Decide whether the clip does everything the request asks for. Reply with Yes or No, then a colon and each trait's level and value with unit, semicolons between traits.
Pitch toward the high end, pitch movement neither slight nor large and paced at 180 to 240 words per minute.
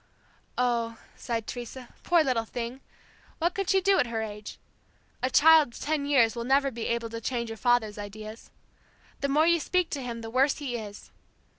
Yes: high, 245 Hz; average, 3.9 semitones; average, 190 wpm